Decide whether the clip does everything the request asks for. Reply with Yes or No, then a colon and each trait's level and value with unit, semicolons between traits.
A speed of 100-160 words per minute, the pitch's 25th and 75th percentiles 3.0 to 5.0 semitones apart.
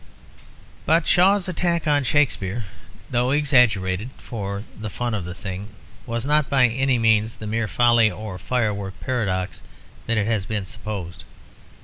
Yes: average, 140 wpm; average, 4.3 semitones